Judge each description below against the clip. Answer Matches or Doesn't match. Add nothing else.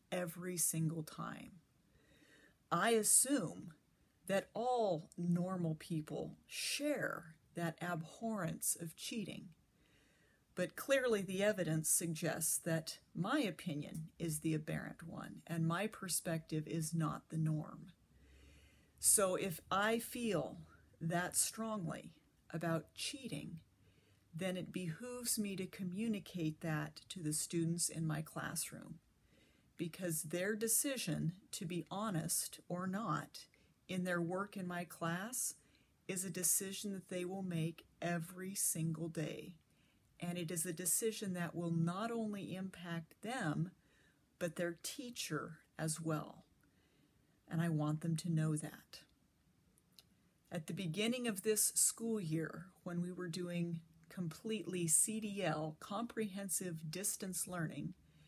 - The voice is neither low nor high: Matches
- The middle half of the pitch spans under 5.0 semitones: Matches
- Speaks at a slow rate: Matches